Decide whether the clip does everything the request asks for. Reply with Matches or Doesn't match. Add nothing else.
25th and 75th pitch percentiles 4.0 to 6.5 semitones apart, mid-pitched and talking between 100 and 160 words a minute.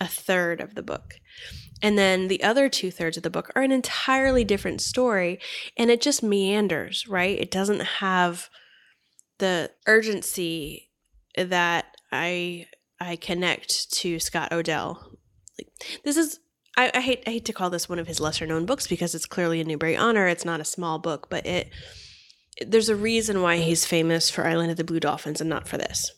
Doesn't match